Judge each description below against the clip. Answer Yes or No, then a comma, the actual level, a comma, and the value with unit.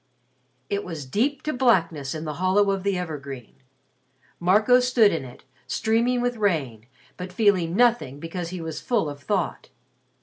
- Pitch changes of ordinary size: No, wide, 6.0 semitones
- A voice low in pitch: No, medium, 185 Hz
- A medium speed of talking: Yes, average, 160 wpm